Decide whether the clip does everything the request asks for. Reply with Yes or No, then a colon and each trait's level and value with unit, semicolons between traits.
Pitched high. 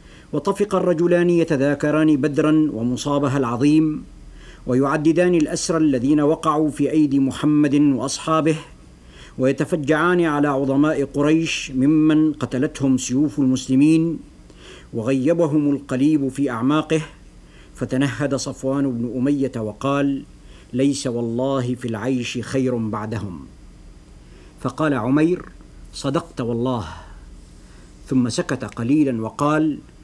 No: medium, 140 Hz